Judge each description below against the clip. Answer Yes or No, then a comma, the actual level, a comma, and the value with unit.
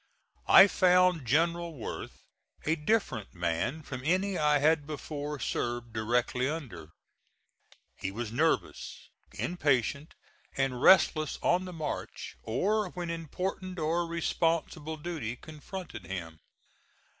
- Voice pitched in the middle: Yes, medium, 155 Hz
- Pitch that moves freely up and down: Yes, wide, 5.8 semitones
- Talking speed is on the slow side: Yes, slow, 110 wpm